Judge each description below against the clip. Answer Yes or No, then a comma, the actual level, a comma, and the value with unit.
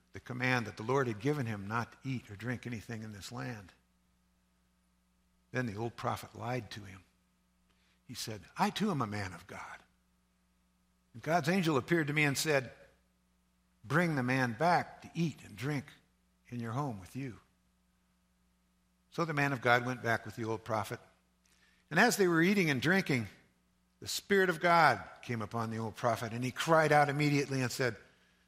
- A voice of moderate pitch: No, low, 115 Hz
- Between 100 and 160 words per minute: No, average, 185 wpm